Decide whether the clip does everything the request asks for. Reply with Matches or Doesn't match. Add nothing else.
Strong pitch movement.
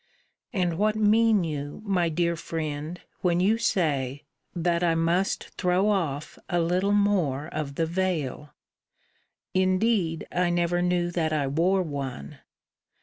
Doesn't match